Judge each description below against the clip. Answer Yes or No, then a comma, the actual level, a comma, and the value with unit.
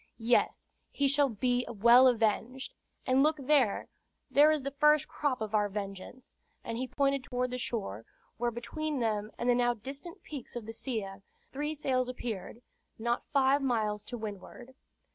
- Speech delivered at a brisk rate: No, average, 165 wpm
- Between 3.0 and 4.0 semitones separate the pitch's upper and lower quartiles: Yes, average, 3.6 semitones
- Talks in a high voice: Yes, high, 245 Hz